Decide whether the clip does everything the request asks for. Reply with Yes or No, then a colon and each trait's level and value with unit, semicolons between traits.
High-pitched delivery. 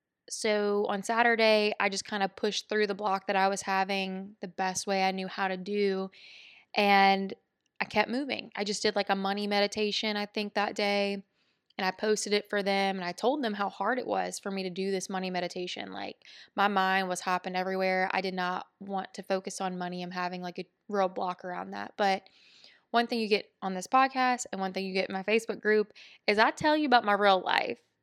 Yes: high, 195 Hz